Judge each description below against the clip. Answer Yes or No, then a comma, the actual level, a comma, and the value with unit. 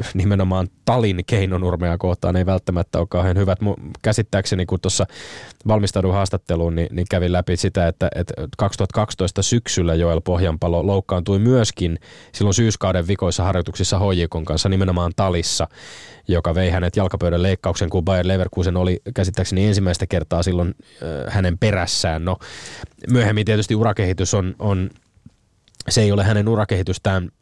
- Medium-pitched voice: No, very low, 95 Hz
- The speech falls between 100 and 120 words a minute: No, average, 135 wpm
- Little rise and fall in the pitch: Yes, narrow, 2.2 semitones